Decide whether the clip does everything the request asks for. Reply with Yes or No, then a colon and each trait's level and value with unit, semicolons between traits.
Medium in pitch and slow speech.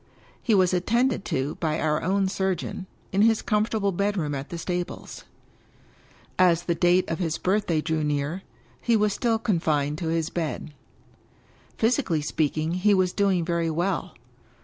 No: medium, 175 Hz; average, 155 wpm